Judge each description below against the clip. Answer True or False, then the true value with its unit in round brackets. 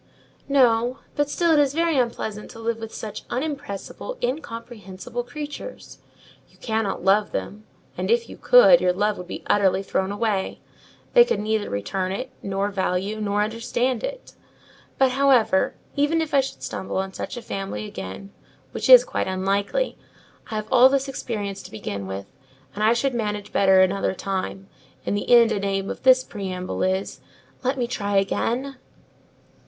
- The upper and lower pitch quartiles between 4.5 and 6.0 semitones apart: True (5.1 semitones)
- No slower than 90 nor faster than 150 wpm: False (170 wpm)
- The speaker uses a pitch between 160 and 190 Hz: False (220 Hz)